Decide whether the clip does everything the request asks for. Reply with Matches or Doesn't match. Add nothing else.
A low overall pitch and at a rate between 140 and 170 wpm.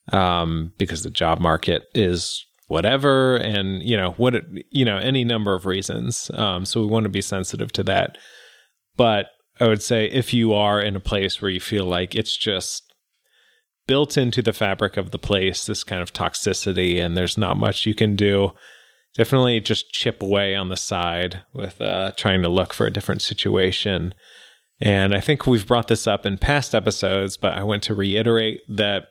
Doesn't match